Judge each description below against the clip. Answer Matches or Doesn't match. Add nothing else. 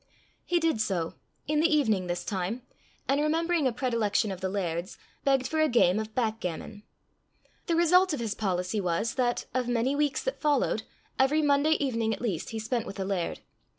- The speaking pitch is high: Matches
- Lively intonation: Matches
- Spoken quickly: Doesn't match